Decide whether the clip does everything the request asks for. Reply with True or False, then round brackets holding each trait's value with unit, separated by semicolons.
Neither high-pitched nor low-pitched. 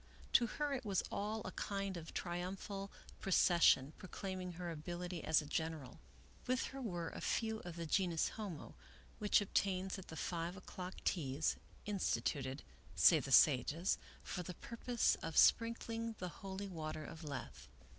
True (180 Hz)